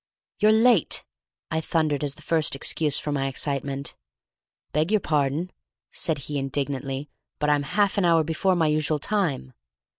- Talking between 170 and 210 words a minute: No, average, 155 wpm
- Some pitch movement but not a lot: Yes, average, 3.1 semitones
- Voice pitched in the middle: Yes, medium, 150 Hz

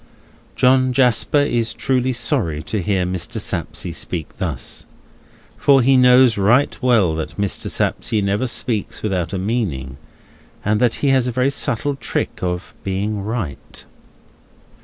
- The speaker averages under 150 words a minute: Yes, average, 140 wpm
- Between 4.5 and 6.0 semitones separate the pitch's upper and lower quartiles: Yes, average, 5.3 semitones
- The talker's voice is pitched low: Yes, low, 110 Hz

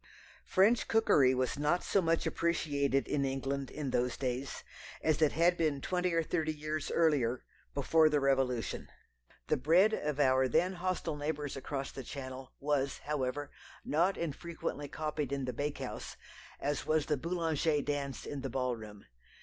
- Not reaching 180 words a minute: Yes, average, 160 wpm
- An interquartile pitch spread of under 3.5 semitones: Yes, average, 3.1 semitones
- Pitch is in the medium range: Yes, medium, 145 Hz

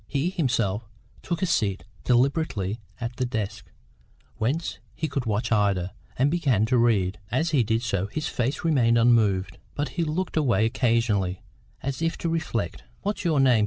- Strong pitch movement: Yes, wide, 6.0 semitones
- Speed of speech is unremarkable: Yes, average, 165 wpm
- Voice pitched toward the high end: No, low, 120 Hz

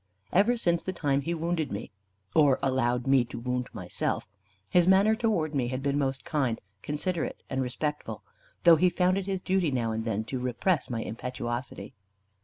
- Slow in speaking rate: No, average, 180 wpm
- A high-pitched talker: No, medium, 140 Hz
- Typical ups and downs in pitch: No, wide, 5.9 semitones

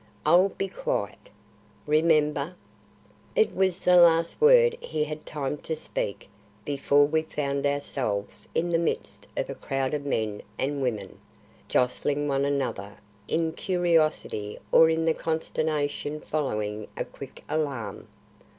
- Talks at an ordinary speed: No, slow, 130 wpm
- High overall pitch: No, medium, 150 Hz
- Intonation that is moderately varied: Yes, average, 3.0 semitones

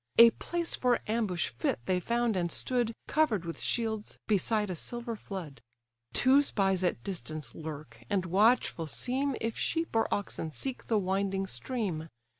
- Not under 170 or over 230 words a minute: No, average, 155 wpm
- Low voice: No, high, 205 Hz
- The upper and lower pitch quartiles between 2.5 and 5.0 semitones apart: No, wide, 5.4 semitones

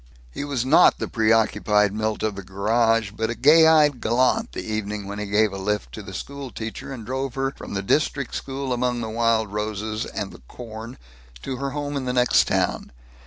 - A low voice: Yes, low, 115 Hz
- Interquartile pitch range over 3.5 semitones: Yes, average, 4.0 semitones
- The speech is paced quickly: Yes, fast, 210 wpm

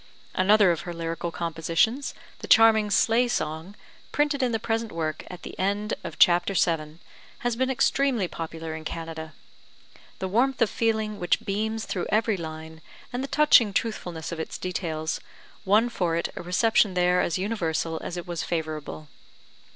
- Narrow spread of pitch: No, wide, 5.4 semitones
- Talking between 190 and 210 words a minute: No, average, 165 wpm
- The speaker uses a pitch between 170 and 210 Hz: Yes, medium, 185 Hz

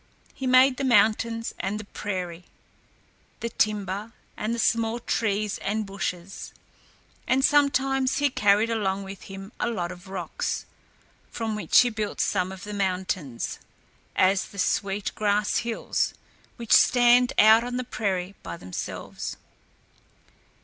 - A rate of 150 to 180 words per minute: No, slow, 135 wpm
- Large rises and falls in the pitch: No, average, 3.3 semitones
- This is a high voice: Yes, high, 210 Hz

